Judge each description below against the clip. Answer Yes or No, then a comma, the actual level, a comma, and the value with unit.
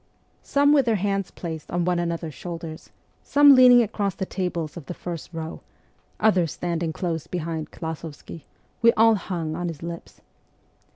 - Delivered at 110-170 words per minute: Yes, average, 165 wpm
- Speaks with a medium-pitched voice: Yes, medium, 175 Hz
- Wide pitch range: No, average, 3.7 semitones